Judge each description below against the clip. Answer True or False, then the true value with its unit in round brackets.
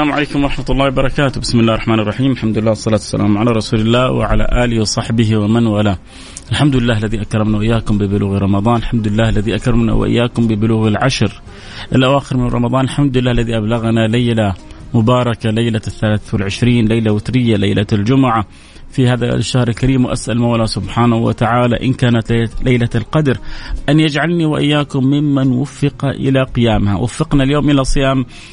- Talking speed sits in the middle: False (155 wpm)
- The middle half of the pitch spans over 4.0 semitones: False (3.1 semitones)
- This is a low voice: True (115 Hz)